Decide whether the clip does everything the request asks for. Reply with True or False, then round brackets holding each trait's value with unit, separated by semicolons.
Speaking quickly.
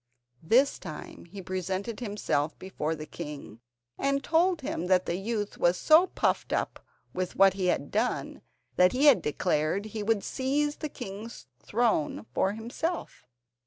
False (155 wpm)